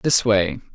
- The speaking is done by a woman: No, male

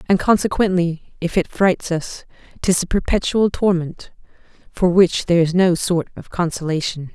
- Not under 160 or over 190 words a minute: No, average, 150 wpm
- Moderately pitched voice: Yes, medium, 175 Hz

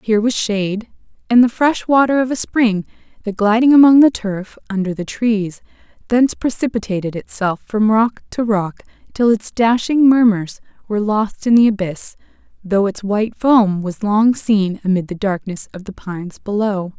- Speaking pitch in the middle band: No, high, 215 Hz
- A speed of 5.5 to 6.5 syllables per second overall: No, 4.9 syllables/s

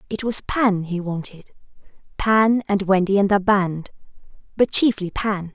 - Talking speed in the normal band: Yes, average, 150 wpm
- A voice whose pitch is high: Yes, high, 200 Hz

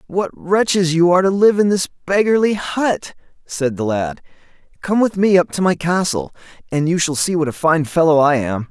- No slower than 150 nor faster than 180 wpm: No, fast, 205 wpm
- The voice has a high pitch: No, medium, 170 Hz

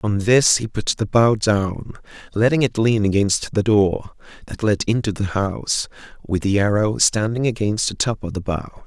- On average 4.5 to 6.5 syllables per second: No, 4.0 syllables/s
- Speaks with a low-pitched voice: Yes, low, 105 Hz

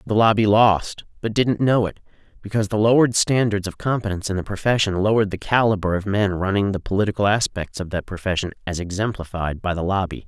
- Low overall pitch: Yes, low, 100 Hz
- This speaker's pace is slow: No, average, 185 wpm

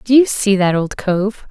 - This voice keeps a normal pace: No, fast, 240 wpm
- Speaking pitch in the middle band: No, high, 205 Hz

